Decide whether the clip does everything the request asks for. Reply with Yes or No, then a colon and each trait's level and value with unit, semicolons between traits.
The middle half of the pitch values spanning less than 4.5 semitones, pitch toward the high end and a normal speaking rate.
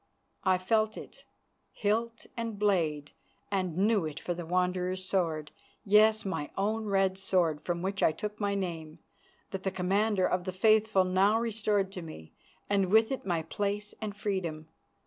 Yes: average, 2.8 semitones; high, 195 Hz; average, 165 wpm